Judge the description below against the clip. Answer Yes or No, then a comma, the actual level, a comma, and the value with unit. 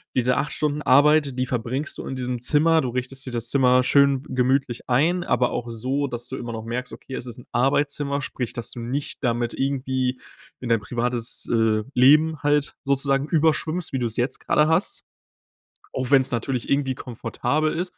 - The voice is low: Yes, low, 130 Hz